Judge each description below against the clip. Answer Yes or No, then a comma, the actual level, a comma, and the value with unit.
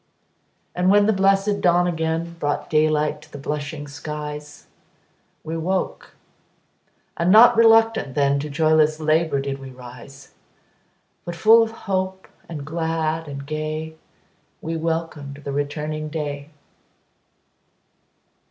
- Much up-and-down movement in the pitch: No, average, 3.0 semitones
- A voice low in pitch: No, medium, 155 Hz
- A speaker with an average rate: No, slow, 120 wpm